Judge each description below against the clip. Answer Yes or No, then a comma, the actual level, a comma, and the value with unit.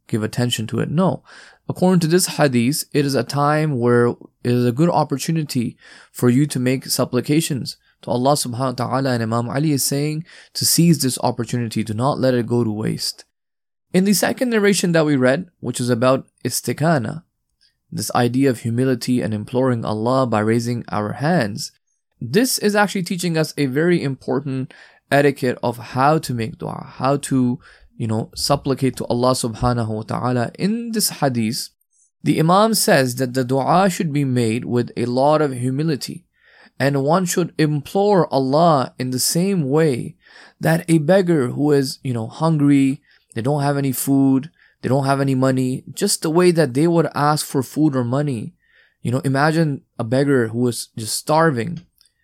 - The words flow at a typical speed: Yes, average, 180 wpm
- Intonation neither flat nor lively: Yes, average, 4.3 semitones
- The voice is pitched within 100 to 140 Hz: Yes, low, 135 Hz